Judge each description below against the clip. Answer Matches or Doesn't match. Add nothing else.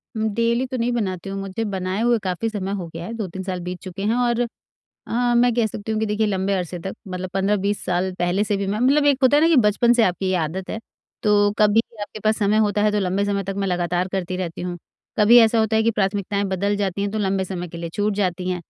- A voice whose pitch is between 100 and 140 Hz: Doesn't match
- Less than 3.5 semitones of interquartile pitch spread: Matches